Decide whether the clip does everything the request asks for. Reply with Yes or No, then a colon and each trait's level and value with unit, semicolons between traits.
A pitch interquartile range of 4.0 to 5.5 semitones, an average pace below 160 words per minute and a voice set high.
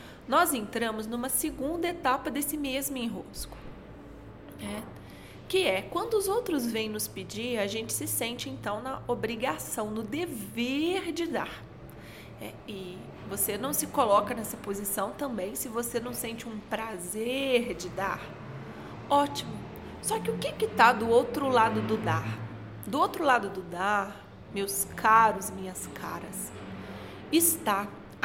Yes: average, 4.9 semitones; average, 140 wpm; high, 235 Hz